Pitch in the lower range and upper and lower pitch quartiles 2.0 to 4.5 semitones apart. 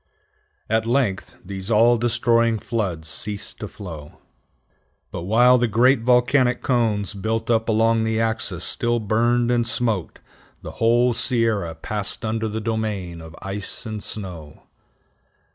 Yes: low, 110 Hz; average, 2.8 semitones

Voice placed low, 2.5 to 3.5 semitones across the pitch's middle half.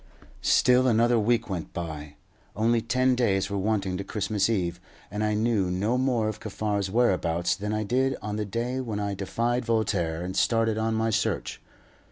Yes: low, 110 Hz; average, 3.2 semitones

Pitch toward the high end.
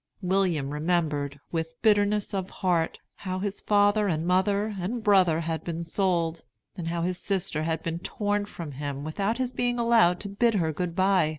No: medium, 180 Hz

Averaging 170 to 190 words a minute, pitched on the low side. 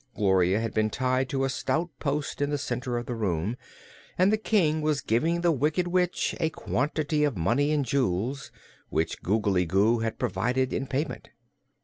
Yes: average, 175 wpm; low, 130 Hz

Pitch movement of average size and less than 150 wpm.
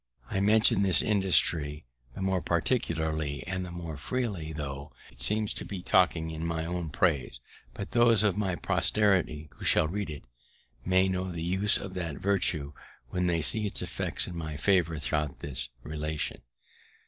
No: average, 3.8 semitones; average, 170 wpm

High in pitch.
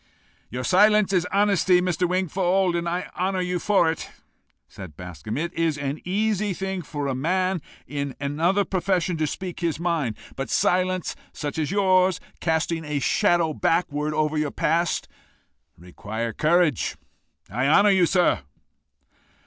No: medium, 170 Hz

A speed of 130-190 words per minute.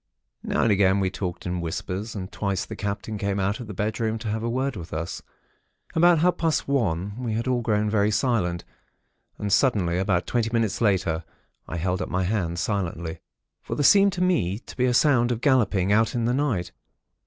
No: fast, 205 wpm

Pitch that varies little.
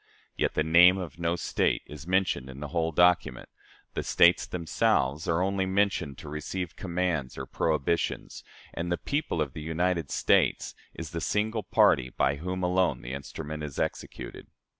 No: average, 3.3 semitones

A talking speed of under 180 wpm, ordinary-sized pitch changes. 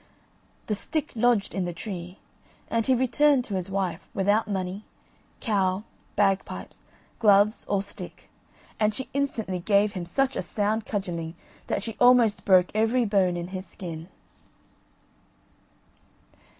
Yes: slow, 135 wpm; average, 3.4 semitones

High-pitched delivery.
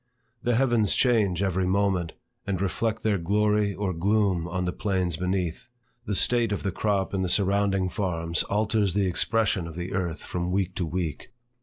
No: very low, 95 Hz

